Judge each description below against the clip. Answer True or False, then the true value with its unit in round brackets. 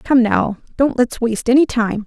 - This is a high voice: True (240 Hz)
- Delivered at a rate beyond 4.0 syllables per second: True (4.9 syllables/s)